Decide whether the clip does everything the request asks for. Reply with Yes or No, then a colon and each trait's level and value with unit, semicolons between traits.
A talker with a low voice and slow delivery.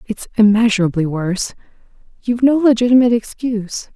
No: high, 220 Hz; slow, 90 wpm